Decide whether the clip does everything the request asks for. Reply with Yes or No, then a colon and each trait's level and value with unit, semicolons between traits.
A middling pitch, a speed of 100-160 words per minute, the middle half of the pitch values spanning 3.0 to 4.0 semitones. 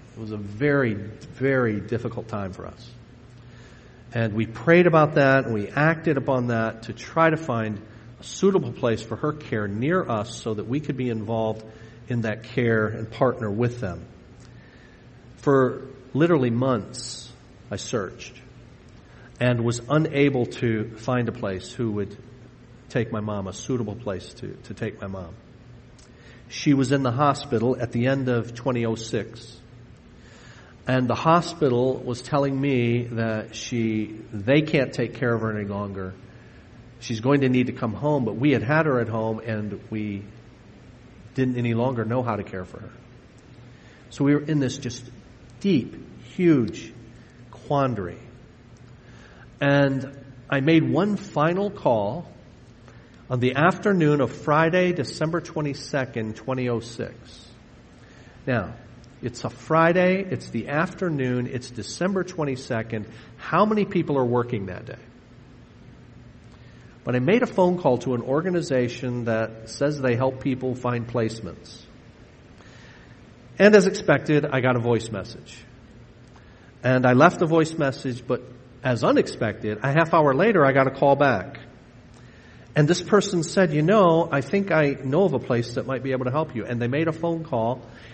No: low, 125 Hz; average, 155 wpm; average, 3.3 semitones